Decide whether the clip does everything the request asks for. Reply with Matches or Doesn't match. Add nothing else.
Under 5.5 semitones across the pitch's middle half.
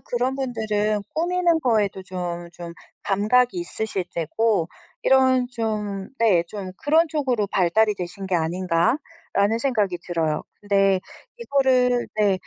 Matches